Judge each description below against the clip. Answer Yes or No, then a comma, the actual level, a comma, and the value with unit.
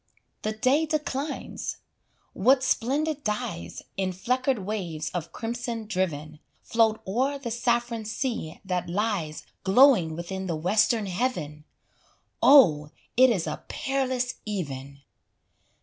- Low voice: No, high, 215 Hz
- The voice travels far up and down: Yes, wide, 6.6 semitones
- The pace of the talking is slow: Yes, slow, 115 wpm